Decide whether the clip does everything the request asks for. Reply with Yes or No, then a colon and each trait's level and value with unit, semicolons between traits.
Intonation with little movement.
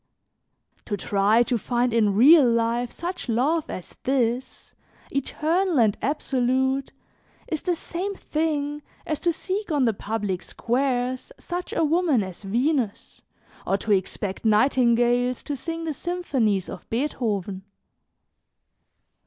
No: wide, 5.4 semitones